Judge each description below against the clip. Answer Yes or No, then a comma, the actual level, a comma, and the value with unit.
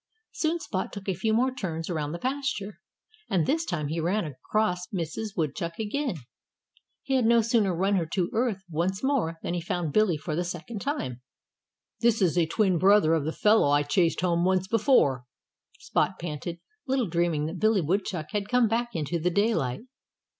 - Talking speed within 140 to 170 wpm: No, average, 185 wpm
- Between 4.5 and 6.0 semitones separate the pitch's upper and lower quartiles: Yes, average, 5.0 semitones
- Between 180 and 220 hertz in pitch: Yes, medium, 185 Hz